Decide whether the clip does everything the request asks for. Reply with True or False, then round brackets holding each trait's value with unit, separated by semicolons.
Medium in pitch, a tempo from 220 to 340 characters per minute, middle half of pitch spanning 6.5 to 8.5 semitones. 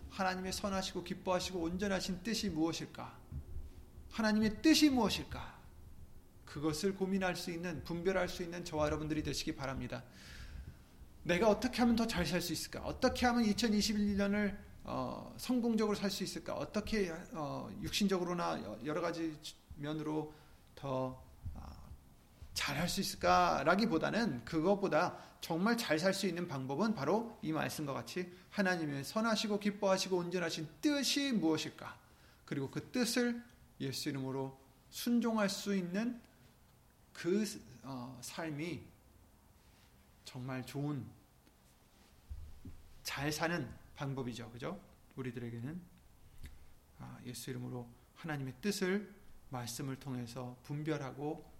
True (165 Hz; 270 characters per minute; 7.1 semitones)